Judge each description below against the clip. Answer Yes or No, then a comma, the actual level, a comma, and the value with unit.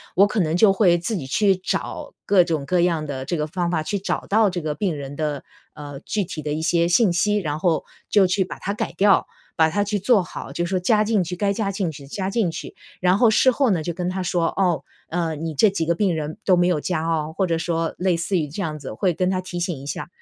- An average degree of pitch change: Yes, average, 3.5 semitones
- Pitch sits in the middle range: Yes, medium, 175 Hz